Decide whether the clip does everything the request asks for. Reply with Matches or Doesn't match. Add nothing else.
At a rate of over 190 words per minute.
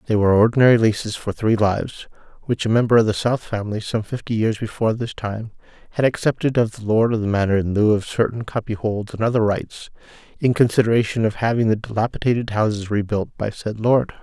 Matches